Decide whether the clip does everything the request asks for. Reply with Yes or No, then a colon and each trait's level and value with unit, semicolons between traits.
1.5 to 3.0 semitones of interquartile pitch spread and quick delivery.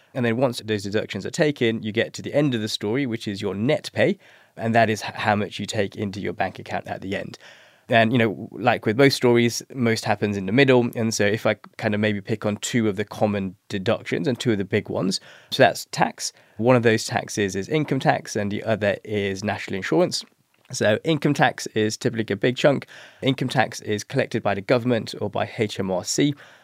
Yes: narrow, 2.6 semitones; fast, 225 wpm